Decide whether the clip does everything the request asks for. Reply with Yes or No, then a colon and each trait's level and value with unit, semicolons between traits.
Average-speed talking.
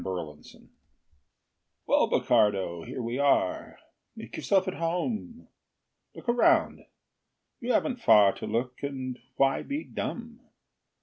No: slow, 115 wpm